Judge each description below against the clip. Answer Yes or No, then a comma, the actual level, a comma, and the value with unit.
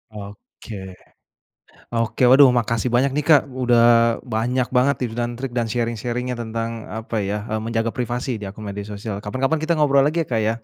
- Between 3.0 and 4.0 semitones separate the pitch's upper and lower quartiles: No, narrow, 2.6 semitones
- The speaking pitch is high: No, low, 120 Hz